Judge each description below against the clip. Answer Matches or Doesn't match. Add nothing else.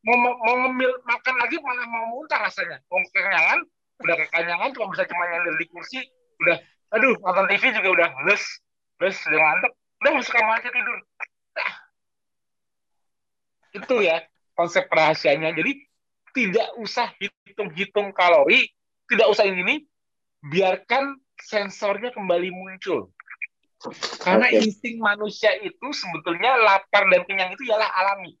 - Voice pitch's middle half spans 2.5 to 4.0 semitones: Doesn't match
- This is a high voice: Matches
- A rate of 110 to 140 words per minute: Matches